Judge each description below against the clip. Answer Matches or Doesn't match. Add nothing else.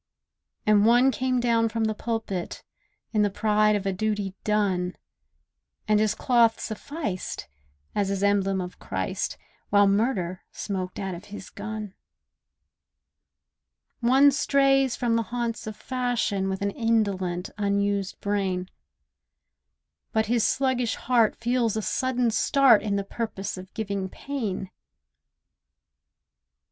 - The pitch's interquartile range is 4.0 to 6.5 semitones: Doesn't match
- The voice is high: Matches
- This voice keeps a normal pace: Doesn't match